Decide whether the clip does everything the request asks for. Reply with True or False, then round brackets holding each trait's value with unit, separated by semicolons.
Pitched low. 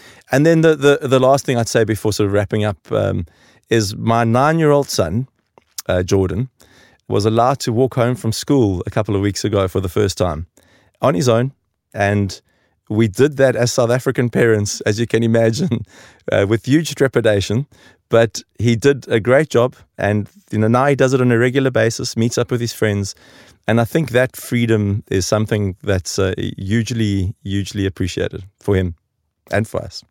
True (115 Hz)